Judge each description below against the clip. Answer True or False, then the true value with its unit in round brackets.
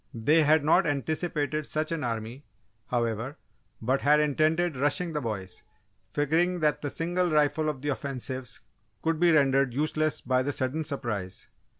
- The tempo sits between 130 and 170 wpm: True (155 wpm)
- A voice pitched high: False (145 Hz)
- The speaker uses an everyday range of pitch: True (3.3 semitones)